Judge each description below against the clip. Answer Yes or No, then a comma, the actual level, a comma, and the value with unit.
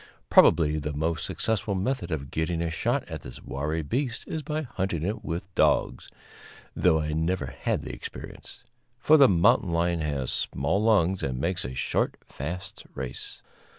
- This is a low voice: Yes, very low, 85 Hz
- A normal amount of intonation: Yes, average, 4.3 semitones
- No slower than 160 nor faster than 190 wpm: Yes, average, 165 wpm